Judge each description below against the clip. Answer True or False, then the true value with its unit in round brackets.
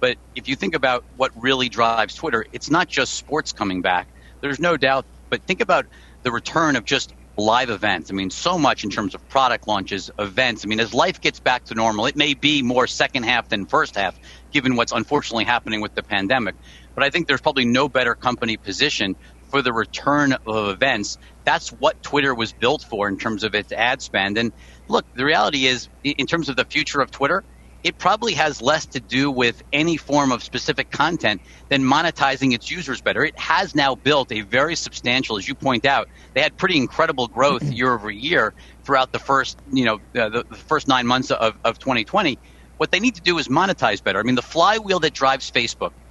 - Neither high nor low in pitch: False (125 Hz)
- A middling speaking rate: False (210 wpm)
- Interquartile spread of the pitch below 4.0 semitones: False (4.7 semitones)